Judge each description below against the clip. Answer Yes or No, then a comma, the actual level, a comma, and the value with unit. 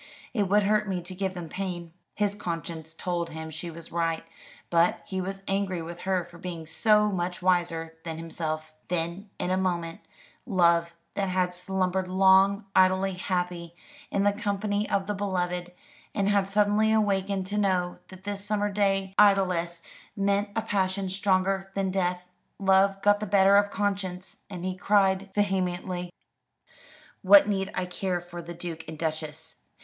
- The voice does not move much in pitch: Yes, narrow, 2.3 semitones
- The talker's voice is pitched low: No, medium, 185 Hz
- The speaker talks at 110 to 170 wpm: Yes, average, 165 wpm